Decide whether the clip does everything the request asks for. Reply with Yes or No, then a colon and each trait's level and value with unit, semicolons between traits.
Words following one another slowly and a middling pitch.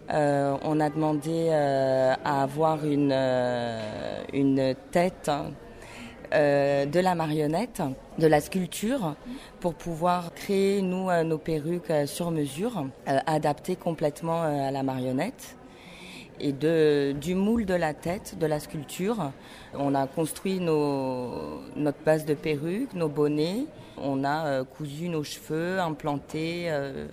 Yes: slow, 140 wpm; medium, 155 Hz